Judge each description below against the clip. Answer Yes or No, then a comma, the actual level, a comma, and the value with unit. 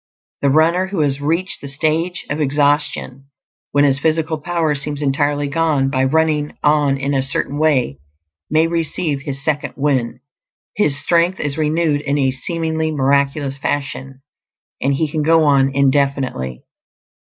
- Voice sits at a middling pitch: Yes, medium, 145 Hz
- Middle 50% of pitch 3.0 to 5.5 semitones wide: No, narrow, 2.5 semitones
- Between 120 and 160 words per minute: Yes, average, 150 wpm